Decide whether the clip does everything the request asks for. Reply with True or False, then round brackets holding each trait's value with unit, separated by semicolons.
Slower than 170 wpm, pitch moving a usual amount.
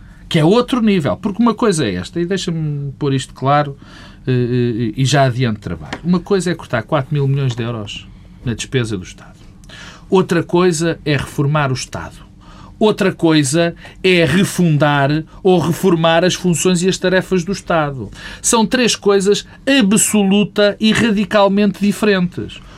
False (150 wpm; 6.2 semitones)